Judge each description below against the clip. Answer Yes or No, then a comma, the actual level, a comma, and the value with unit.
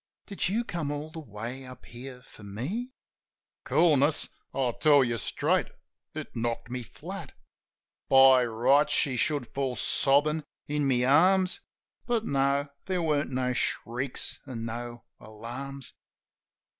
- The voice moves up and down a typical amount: Yes, average, 3.8 semitones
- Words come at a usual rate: No, slow, 130 wpm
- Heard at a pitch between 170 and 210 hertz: No, low, 135 Hz